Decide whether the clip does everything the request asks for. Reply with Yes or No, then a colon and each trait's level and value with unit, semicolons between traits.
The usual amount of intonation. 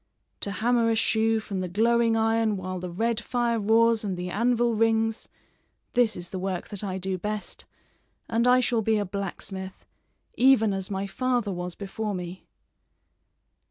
Yes: average, 3.3 semitones